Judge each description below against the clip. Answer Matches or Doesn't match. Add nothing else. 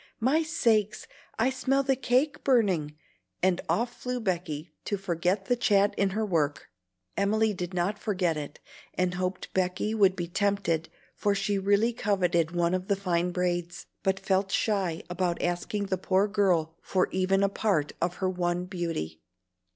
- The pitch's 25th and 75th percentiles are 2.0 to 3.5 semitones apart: Matches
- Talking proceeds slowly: Doesn't match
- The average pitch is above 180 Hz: Matches